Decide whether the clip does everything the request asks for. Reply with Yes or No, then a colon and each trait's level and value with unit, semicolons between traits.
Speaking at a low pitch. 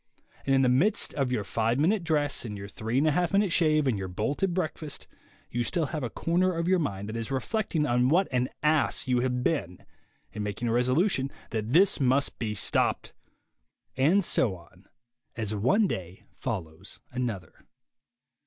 Yes: low, 130 Hz